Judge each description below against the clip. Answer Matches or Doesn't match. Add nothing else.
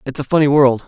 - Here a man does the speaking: Matches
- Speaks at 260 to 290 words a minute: Matches